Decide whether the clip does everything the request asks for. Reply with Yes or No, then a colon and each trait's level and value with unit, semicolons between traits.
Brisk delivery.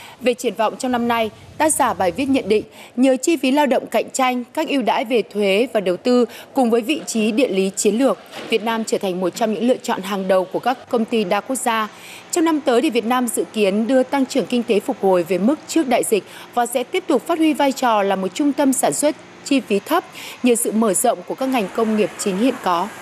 Yes: fast, 265 wpm